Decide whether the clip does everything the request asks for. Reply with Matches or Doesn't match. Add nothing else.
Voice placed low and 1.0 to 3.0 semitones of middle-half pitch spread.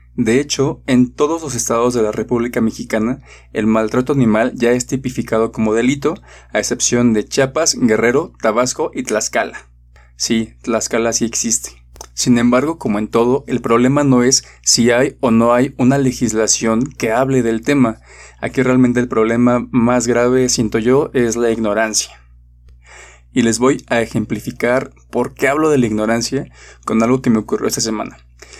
Matches